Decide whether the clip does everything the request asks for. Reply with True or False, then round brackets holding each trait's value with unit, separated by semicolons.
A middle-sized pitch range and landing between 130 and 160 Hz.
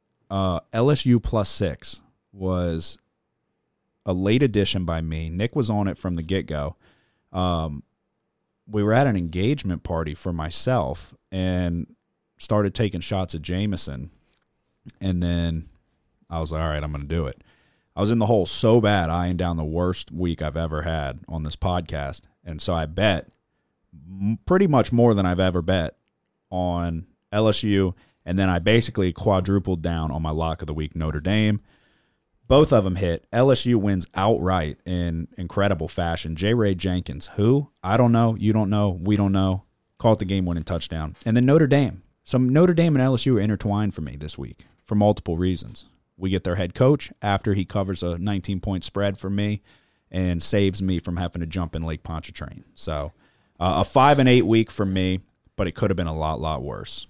False (3.9 semitones; 95 Hz)